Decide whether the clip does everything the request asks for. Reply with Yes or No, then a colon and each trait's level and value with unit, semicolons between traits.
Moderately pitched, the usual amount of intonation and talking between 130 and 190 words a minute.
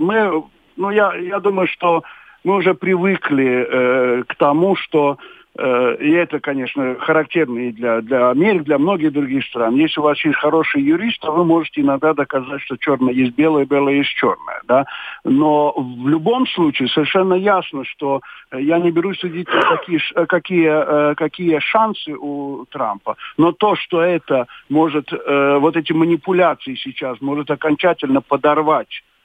Yes: medium, 155 Hz; average, 4.2 semitones; fast, 160 wpm